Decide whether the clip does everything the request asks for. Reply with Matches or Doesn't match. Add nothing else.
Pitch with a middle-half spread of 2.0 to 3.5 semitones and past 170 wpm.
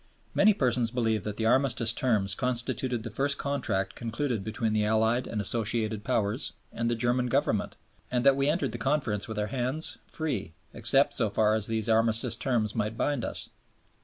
Matches